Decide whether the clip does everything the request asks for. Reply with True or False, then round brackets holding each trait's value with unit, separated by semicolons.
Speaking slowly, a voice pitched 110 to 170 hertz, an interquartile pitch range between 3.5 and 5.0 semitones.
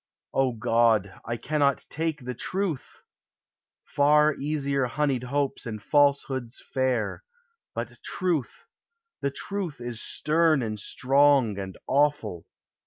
True (110 wpm; 140 Hz; 3.8 semitones)